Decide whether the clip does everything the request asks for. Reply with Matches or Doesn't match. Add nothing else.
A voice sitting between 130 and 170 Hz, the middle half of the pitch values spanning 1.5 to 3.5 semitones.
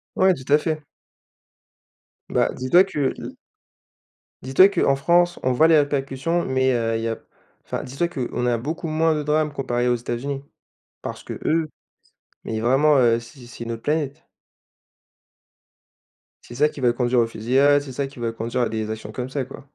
Doesn't match